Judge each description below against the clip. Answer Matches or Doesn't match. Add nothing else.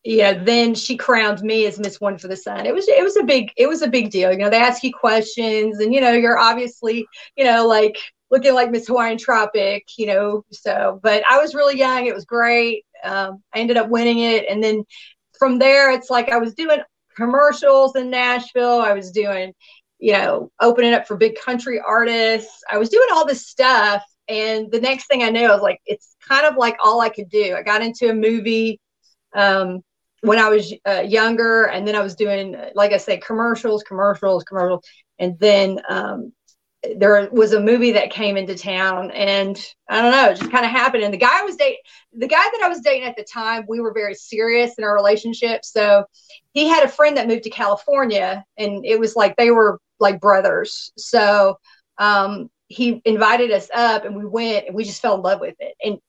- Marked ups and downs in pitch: Doesn't match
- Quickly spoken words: Matches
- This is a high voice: Matches